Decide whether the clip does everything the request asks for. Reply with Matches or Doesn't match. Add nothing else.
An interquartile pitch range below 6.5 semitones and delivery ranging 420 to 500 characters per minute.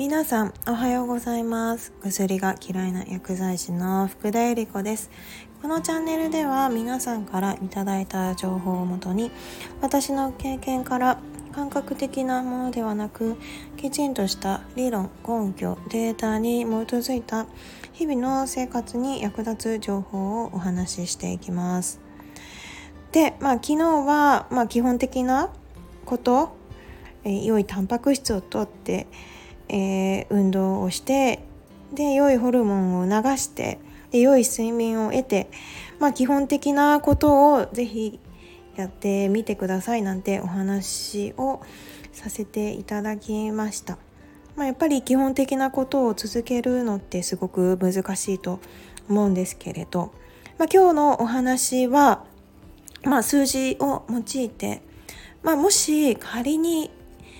Doesn't match